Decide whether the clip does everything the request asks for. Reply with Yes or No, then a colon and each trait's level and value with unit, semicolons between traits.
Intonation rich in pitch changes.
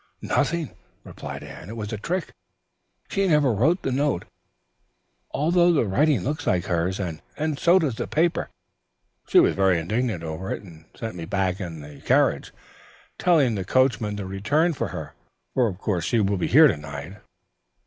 Yes: wide, 8.5 semitones